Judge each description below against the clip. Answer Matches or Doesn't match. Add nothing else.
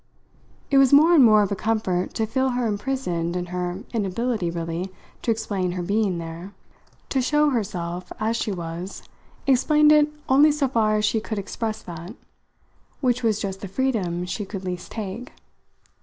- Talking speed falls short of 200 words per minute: Matches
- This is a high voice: Matches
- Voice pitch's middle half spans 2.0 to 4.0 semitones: Doesn't match